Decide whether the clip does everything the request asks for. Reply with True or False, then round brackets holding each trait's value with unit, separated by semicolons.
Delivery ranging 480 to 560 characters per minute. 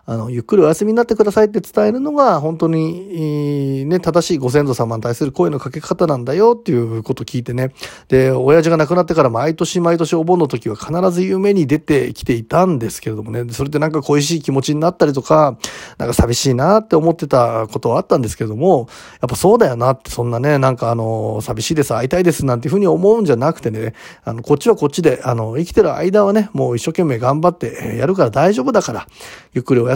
True (490 characters per minute)